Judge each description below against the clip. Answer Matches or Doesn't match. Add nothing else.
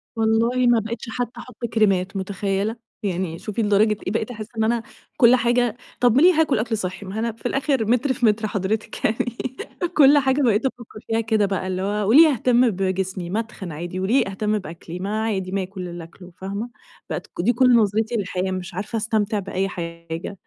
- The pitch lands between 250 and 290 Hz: Doesn't match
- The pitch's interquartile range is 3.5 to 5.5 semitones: Matches